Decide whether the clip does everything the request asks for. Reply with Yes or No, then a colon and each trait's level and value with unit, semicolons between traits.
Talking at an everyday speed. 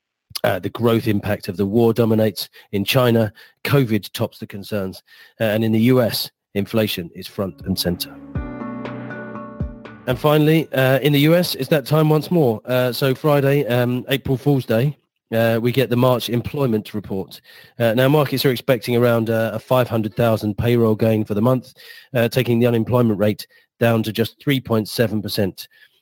Yes: average, 165 wpm